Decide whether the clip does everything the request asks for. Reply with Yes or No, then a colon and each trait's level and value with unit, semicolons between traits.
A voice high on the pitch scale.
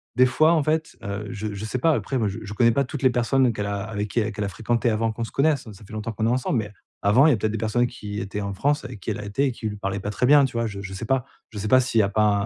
No: low, 110 Hz